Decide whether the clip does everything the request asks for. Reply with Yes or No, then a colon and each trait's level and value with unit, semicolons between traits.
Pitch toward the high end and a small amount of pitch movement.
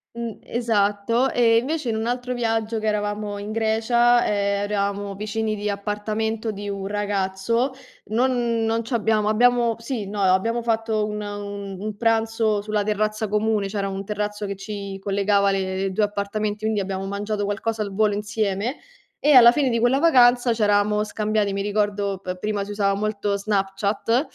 Yes: high, 210 Hz; narrow, 2.0 semitones